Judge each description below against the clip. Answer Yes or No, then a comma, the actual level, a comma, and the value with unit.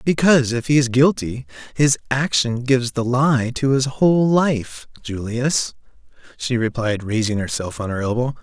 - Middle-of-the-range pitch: No, low, 125 Hz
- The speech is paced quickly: No, average, 155 wpm